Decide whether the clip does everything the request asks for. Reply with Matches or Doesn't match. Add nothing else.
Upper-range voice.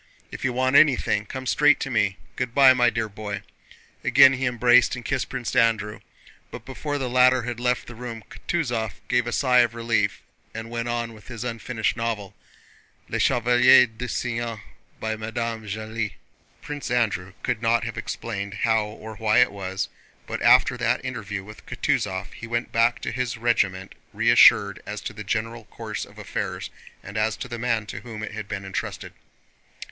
Doesn't match